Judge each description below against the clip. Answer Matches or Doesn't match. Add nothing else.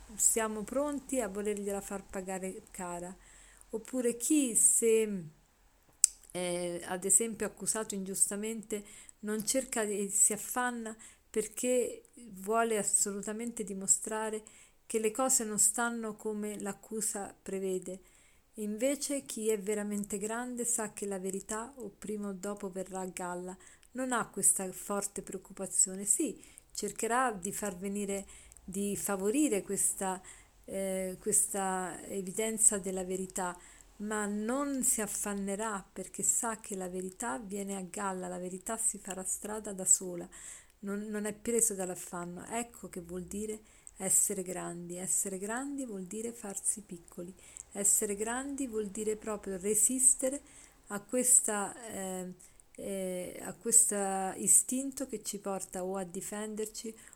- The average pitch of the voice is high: Matches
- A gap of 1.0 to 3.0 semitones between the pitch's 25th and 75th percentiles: Matches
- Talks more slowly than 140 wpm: Matches